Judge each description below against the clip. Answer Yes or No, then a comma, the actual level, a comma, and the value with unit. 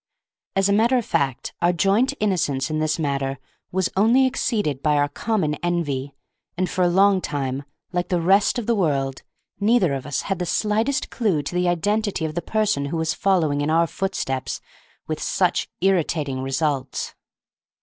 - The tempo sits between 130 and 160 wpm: No, average, 175 wpm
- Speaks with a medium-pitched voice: Yes, medium, 175 Hz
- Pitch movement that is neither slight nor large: No, wide, 5.7 semitones